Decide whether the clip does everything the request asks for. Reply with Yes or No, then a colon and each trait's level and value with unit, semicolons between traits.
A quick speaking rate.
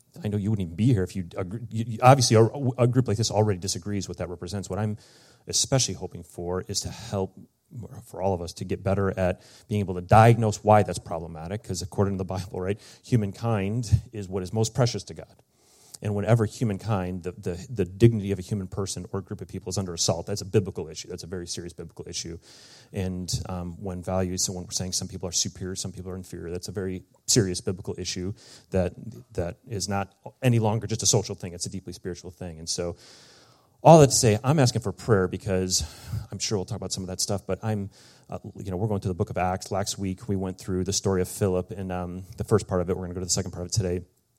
Yes: fast, 245 wpm